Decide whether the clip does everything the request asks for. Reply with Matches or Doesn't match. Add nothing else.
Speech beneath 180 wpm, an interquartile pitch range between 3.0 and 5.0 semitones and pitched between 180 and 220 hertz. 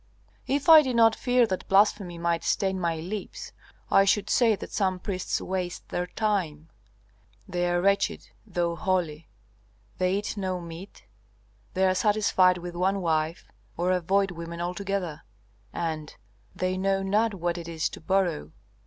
Doesn't match